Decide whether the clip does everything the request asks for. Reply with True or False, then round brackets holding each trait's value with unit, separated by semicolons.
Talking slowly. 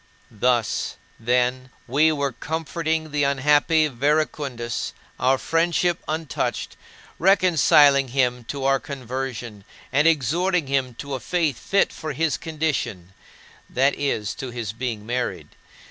True (120 wpm)